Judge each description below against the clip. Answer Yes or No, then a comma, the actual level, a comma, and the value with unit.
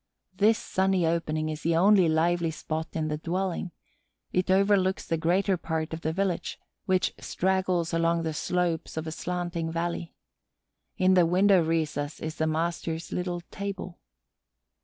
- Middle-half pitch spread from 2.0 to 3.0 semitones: Yes, narrow, 2.5 semitones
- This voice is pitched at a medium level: Yes, medium, 170 Hz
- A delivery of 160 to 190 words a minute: No, average, 150 wpm